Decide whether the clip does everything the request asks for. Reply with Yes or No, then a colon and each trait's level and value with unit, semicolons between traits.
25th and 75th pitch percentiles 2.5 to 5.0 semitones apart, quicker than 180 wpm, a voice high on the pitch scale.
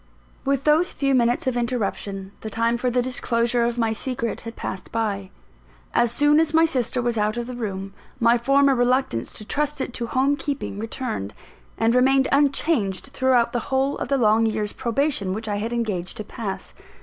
Yes: average, 3.4 semitones; average, 190 wpm; high, 240 Hz